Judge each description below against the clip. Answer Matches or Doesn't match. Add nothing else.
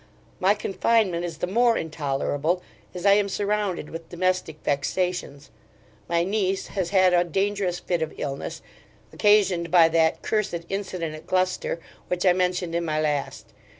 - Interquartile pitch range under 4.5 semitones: Matches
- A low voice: Doesn't match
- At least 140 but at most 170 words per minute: Matches